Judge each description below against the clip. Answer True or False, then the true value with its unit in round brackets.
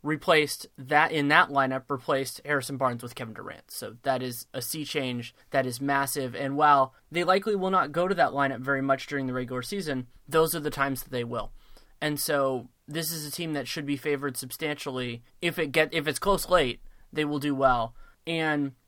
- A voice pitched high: False (140 Hz)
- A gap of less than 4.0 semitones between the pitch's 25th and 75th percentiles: True (2.9 semitones)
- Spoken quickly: True (210 wpm)